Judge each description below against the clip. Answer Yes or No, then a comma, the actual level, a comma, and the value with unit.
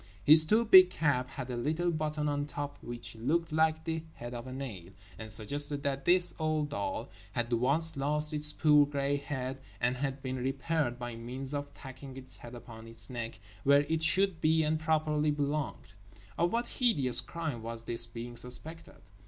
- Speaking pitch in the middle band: Yes, medium, 145 Hz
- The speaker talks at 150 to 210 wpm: Yes, average, 185 wpm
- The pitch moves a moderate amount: Yes, average, 4.0 semitones